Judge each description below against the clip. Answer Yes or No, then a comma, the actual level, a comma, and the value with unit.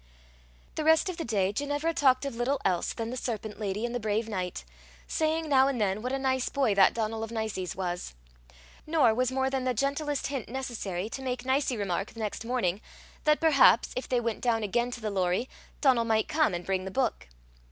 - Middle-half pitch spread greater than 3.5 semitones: Yes, average, 4.2 semitones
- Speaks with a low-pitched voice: No, high, 240 Hz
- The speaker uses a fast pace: Yes, fast, 215 wpm